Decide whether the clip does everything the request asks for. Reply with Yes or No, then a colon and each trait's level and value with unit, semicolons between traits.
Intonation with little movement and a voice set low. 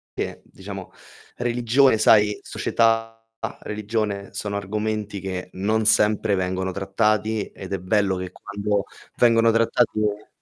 Yes: narrow, 2.1 semitones; low, 105 Hz